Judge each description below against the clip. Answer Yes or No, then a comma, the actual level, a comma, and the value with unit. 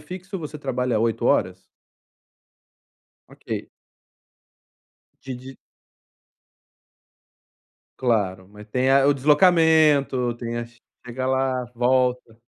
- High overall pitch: No, low, 130 Hz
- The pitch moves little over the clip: No, average, 3.3 semitones